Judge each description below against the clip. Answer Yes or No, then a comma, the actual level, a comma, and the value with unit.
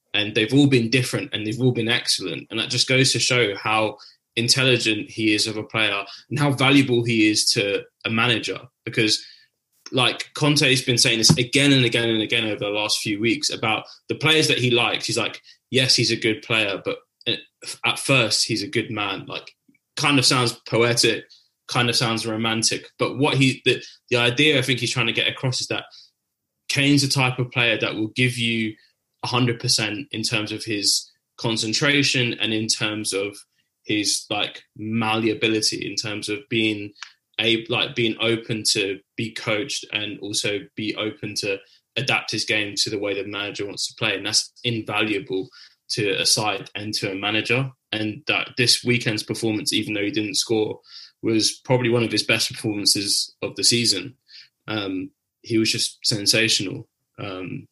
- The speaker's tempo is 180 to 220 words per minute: Yes, average, 185 wpm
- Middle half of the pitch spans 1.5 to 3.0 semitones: Yes, average, 2.7 semitones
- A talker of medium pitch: No, low, 115 Hz